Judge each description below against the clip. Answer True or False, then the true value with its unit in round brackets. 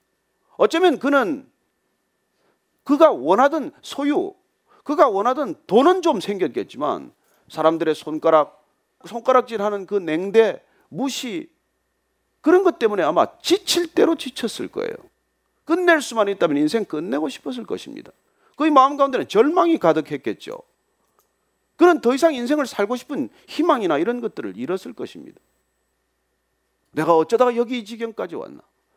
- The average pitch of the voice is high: True (260 Hz)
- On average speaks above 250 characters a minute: True (290 characters per minute)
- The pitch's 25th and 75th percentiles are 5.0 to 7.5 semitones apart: False (8.4 semitones)